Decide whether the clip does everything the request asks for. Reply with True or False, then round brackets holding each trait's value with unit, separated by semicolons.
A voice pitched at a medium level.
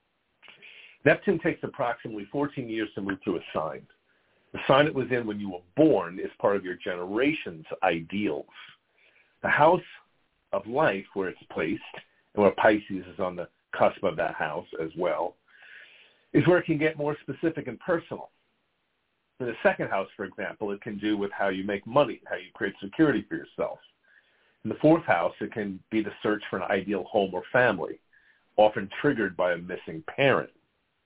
False (110 Hz)